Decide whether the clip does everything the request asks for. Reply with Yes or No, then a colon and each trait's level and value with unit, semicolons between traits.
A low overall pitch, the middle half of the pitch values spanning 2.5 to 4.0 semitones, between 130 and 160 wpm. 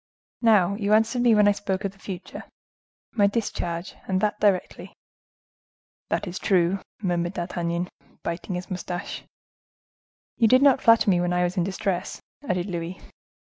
No: high, 190 Hz; average, 2.9 semitones; average, 150 wpm